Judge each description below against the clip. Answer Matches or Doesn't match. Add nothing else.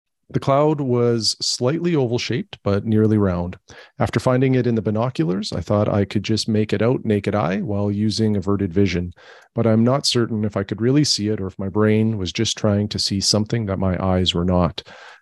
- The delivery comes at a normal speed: Doesn't match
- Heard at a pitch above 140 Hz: Doesn't match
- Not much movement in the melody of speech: Doesn't match